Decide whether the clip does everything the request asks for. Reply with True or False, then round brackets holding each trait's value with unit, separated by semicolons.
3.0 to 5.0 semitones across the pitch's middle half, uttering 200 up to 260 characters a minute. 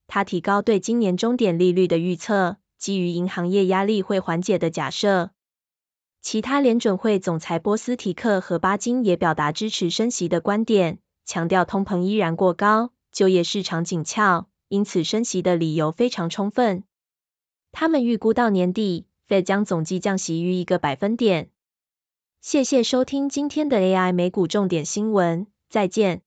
True (3.5 semitones; 255 characters per minute)